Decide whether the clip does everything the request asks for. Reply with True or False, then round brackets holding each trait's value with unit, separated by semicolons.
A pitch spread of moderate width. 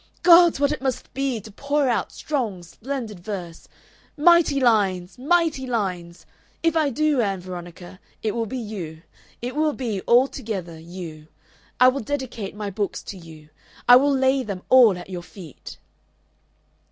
False (7.0 semitones)